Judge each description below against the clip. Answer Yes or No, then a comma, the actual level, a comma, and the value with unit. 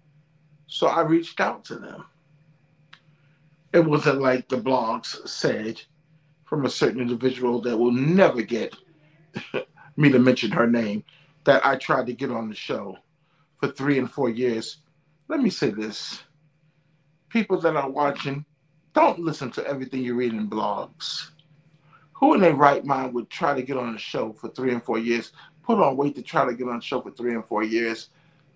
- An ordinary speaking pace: Yes, average, 180 wpm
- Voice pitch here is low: No, medium, 145 Hz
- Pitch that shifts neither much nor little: Yes, average, 3.9 semitones